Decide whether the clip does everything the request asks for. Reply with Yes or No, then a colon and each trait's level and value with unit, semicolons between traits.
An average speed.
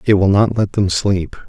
No: fast, 245 wpm